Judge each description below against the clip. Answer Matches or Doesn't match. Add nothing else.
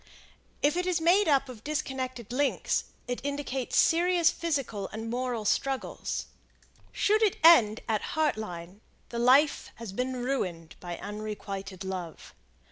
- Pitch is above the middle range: Matches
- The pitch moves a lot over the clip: Matches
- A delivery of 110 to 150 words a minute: Matches